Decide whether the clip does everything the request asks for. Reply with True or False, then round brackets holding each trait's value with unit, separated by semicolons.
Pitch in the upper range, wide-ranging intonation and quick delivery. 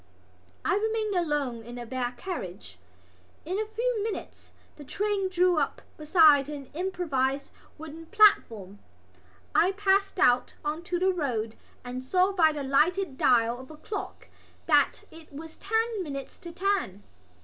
False (320 Hz; 6.6 semitones; 150 wpm)